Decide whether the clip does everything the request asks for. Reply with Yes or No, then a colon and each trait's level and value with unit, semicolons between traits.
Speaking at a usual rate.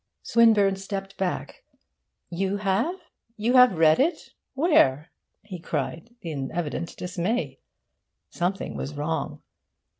No: slow, 110 wpm